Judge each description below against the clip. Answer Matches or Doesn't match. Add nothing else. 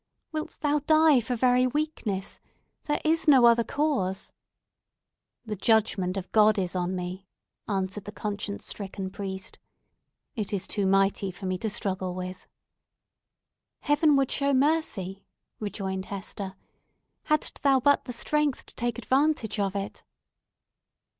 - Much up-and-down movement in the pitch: Matches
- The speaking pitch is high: Matches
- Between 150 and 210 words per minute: Doesn't match